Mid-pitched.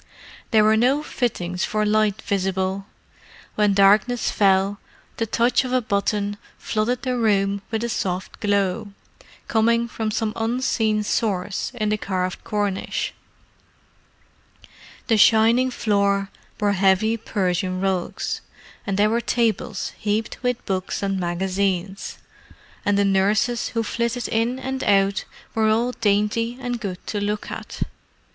No: high, 210 Hz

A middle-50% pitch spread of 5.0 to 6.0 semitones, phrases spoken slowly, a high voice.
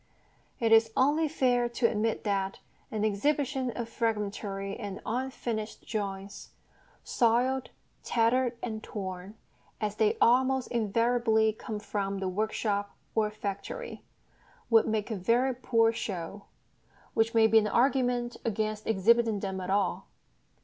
No: average, 2.8 semitones; slow, 130 wpm; high, 225 Hz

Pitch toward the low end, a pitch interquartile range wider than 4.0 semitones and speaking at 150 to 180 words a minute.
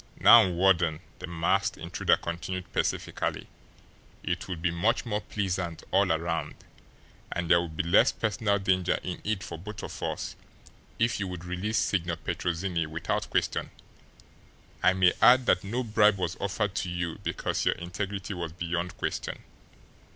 No: very low, 90 Hz; average, 2.8 semitones; average, 155 wpm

